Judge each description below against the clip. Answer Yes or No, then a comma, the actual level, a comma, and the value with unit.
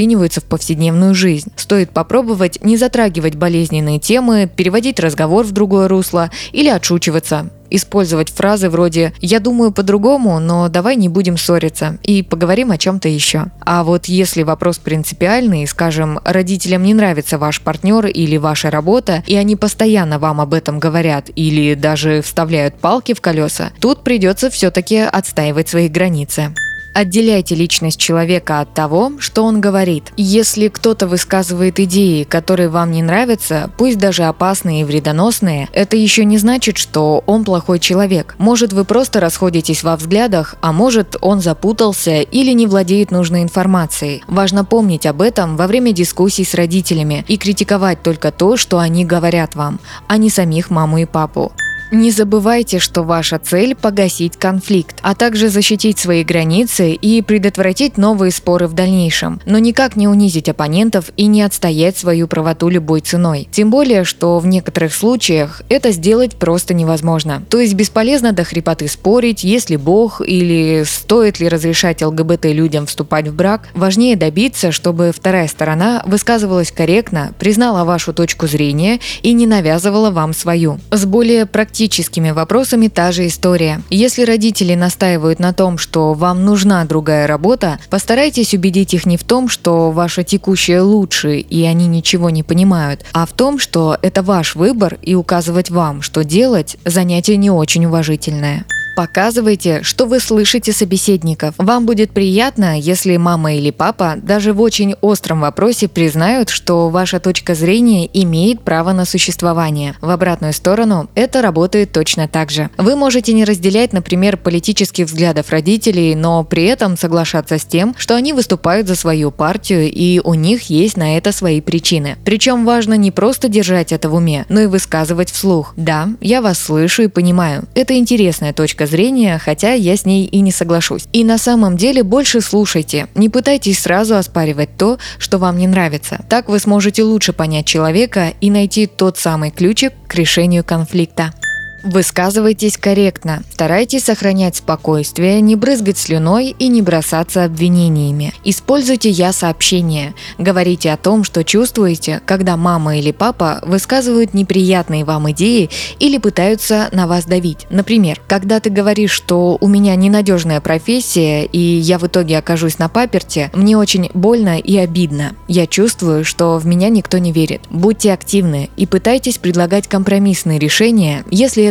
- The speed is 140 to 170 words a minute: Yes, average, 155 wpm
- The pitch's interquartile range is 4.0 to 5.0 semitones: Yes, average, 4.3 semitones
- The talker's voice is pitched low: No, medium, 185 Hz